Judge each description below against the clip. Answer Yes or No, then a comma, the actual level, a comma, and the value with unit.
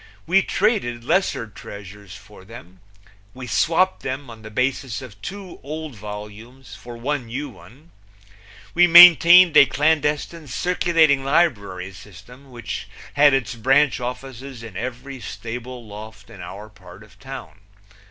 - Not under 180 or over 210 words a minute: No, slow, 135 wpm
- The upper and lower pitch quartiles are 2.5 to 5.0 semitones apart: No, wide, 5.5 semitones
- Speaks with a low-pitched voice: Yes, low, 125 Hz